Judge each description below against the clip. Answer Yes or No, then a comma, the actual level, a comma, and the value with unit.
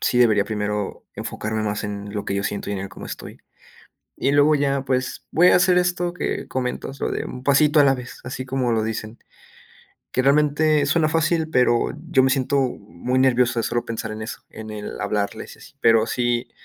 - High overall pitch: No, low, 125 Hz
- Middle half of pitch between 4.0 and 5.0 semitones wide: Yes, average, 4.7 semitones